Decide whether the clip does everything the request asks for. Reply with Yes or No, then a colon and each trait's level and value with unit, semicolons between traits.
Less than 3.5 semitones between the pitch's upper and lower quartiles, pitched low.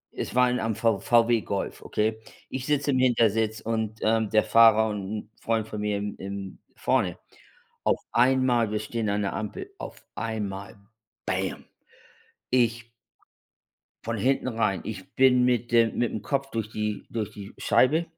Yes: narrow, 2.4 semitones; low, 110 Hz